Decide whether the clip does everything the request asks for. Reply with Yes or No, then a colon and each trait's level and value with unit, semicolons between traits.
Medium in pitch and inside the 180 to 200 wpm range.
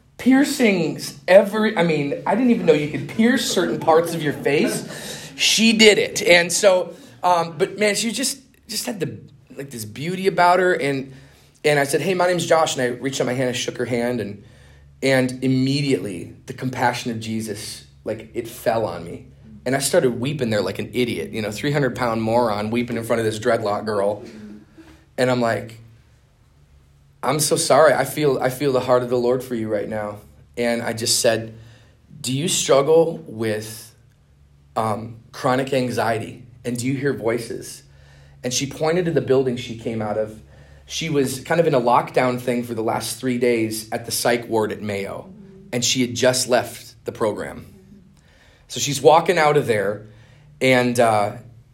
No: low, 125 Hz; average, 190 wpm